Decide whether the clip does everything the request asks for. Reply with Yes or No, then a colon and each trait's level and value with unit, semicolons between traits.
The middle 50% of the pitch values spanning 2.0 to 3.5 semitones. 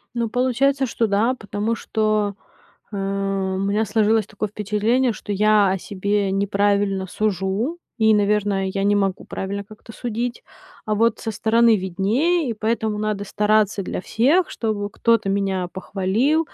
Yes: narrow, 2.4 semitones